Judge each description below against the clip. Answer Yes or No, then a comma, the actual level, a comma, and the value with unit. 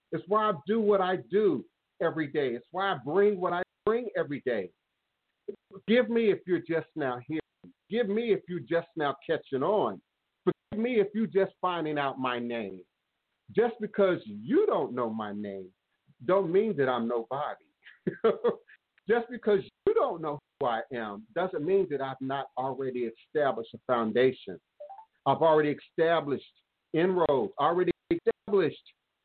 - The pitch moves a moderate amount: No, wide, 7.9 semitones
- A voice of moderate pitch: Yes, medium, 180 Hz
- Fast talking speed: No, average, 160 wpm